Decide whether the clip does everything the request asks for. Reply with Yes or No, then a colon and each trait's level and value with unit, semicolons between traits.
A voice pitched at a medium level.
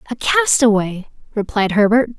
No: high, 220 Hz